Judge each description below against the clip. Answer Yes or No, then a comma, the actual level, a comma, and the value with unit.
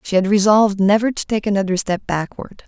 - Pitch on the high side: Yes, high, 200 Hz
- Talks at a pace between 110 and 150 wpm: No, average, 200 wpm